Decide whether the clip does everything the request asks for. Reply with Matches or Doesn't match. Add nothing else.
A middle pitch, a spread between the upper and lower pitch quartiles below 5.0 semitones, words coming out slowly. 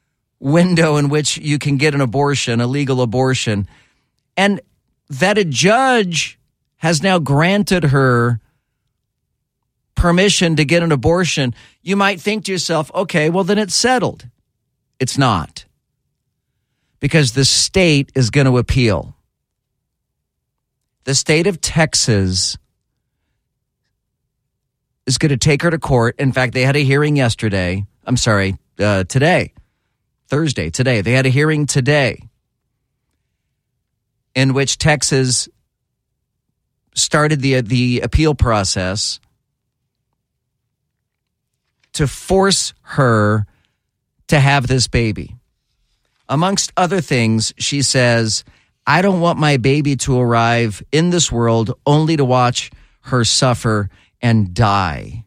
Doesn't match